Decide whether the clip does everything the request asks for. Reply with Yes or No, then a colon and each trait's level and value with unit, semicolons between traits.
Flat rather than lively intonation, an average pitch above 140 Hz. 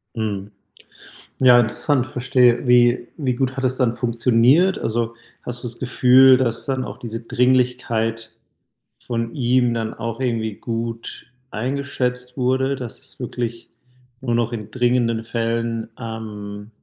No: narrow, 1.8 semitones; low, 120 Hz